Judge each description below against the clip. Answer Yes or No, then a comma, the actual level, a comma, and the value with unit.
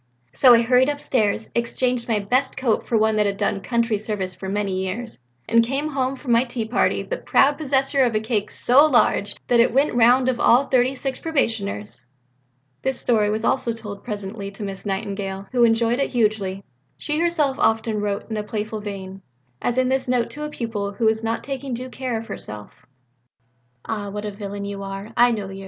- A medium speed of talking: No, fast, 210 wpm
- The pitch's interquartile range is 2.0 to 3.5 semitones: No, average, 3.9 semitones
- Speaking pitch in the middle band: No, high, 225 Hz